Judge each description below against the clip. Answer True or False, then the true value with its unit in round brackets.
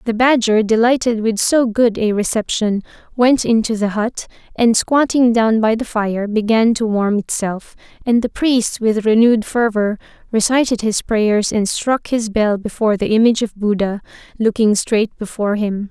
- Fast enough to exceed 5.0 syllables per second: False (4.7 syllables/s)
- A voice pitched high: True (220 Hz)